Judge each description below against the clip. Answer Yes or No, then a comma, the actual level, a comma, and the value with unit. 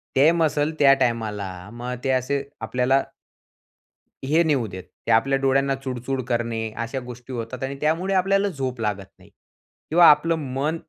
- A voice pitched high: No, low, 135 Hz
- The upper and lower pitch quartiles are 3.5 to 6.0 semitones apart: Yes, average, 4.0 semitones